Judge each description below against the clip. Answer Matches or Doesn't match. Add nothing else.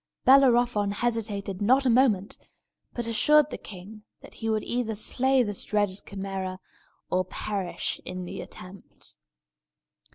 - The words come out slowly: Matches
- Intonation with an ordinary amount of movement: Matches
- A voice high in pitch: Matches